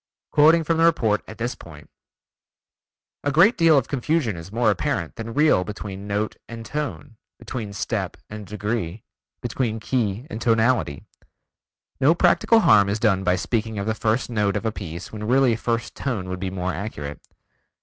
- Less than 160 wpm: No, average, 170 wpm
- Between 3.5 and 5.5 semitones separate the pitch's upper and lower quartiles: Yes, average, 4.3 semitones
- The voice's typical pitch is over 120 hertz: No, low, 110 Hz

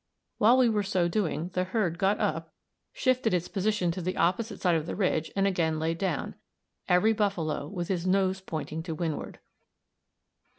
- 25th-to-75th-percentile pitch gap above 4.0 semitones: No, average, 3.5 semitones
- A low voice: No, medium, 185 Hz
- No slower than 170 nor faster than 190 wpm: Yes, average, 175 wpm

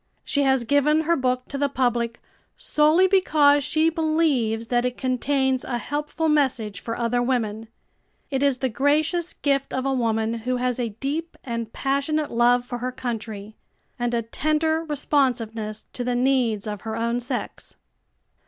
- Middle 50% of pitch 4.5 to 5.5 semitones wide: No, average, 3.8 semitones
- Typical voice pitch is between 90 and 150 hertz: No, very high, 255 Hz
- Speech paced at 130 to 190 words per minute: Yes, average, 160 wpm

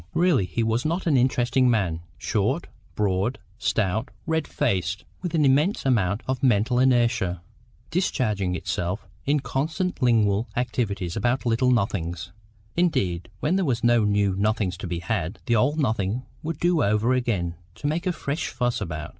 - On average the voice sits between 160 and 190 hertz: No, low, 120 Hz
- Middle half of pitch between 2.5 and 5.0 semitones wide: No, wide, 5.6 semitones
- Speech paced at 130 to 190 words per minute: Yes, average, 160 wpm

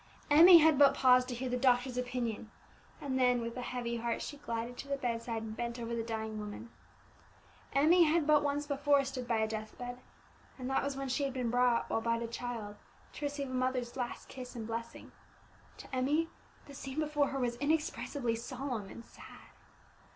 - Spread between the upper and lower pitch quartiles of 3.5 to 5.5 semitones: No, average, 3.1 semitones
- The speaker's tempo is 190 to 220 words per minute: Yes, average, 200 wpm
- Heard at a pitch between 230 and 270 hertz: Yes, very high, 250 Hz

